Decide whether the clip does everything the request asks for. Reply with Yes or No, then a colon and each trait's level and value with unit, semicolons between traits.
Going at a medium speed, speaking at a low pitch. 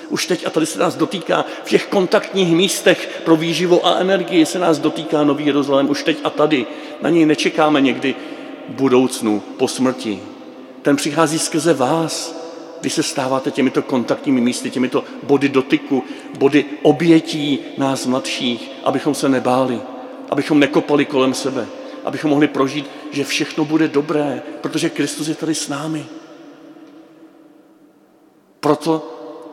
No: average, 140 wpm; medium, 150 Hz